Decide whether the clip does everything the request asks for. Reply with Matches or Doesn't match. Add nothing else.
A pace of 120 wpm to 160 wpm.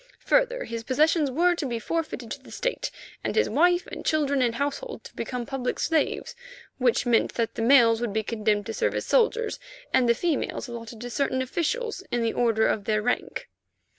Doesn't match